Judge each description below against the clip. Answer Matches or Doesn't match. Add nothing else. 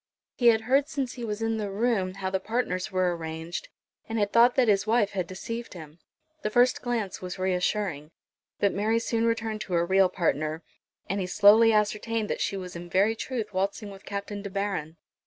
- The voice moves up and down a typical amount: Matches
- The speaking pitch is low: Doesn't match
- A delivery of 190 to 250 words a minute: Matches